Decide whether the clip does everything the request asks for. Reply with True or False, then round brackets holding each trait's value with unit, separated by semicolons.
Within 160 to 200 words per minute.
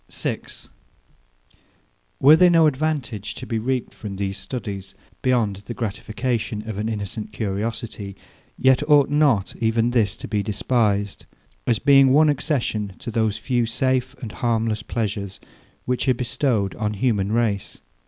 False (145 wpm)